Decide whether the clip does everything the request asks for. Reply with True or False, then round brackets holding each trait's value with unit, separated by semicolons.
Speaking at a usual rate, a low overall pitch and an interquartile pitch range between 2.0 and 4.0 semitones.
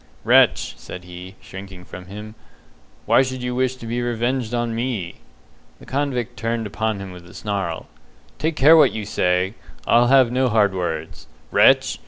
False (170 wpm; 110 Hz; 4.8 semitones)